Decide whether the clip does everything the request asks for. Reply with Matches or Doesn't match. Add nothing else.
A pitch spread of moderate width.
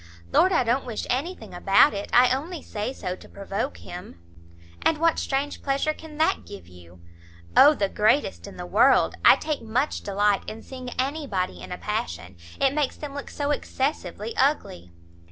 Doesn't match